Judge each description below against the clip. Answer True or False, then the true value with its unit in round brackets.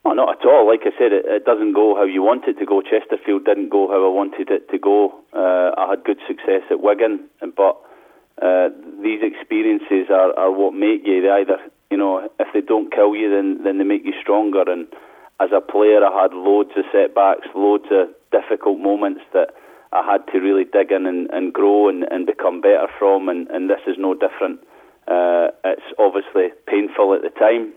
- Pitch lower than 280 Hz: False (310 Hz)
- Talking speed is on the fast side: True (210 wpm)